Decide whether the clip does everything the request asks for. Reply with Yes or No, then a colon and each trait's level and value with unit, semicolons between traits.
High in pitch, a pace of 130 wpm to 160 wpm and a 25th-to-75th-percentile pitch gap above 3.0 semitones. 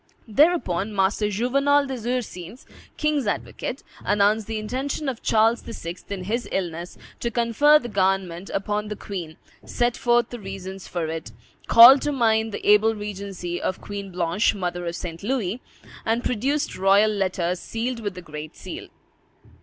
Yes: high, 210 Hz; average, 155 wpm; average, 4.4 semitones